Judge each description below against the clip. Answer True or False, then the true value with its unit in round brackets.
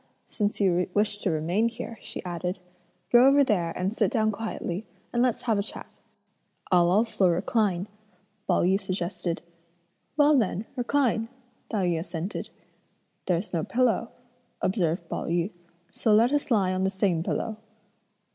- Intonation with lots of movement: False (4.2 semitones)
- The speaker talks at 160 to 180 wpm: False (150 wpm)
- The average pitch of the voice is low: False (200 Hz)